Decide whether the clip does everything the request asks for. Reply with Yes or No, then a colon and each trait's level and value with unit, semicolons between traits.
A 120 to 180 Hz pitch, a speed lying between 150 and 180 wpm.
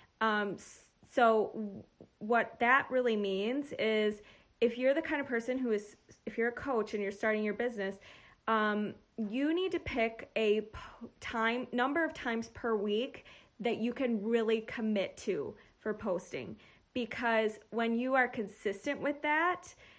No: high, 230 Hz; average, 155 wpm